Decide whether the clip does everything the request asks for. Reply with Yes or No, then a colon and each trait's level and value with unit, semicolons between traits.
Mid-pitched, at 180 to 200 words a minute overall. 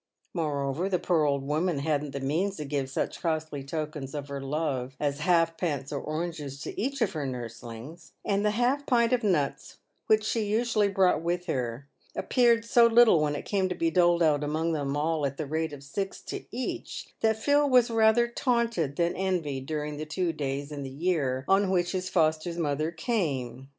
Yes: medium, 160 Hz; average, 195 wpm